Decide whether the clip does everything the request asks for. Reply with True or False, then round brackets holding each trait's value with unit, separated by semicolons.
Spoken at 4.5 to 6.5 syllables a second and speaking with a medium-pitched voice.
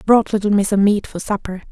False (5.9 syllables/s; 200 Hz)